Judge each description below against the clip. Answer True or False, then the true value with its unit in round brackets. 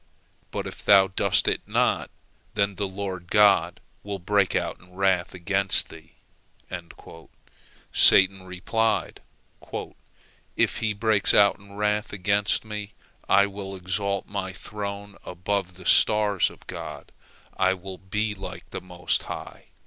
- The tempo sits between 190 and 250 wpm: False (135 wpm)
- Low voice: True (100 Hz)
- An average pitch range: False (1.7 semitones)